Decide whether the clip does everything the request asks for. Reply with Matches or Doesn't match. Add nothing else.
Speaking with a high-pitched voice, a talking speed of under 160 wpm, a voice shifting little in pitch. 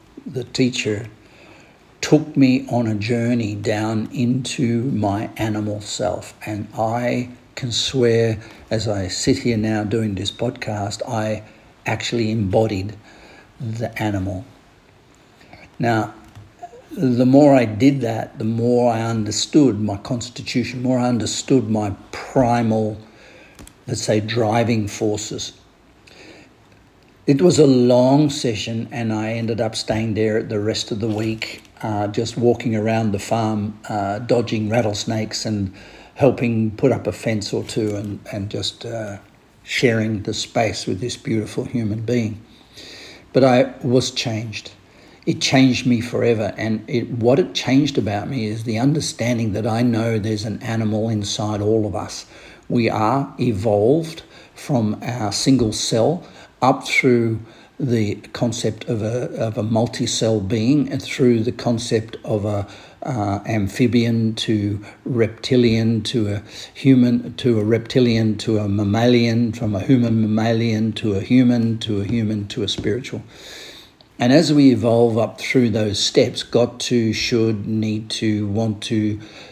Doesn't match